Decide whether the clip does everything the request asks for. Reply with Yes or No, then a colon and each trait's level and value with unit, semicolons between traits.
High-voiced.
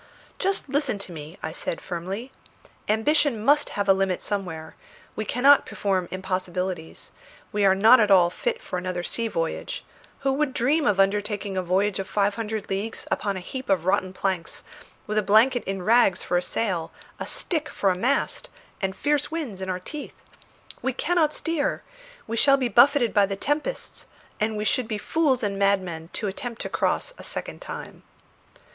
Yes: high, 205 Hz